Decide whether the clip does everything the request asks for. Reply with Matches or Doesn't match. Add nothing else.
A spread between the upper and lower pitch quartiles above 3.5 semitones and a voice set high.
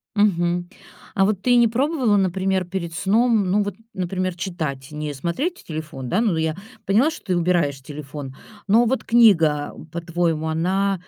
Doesn't match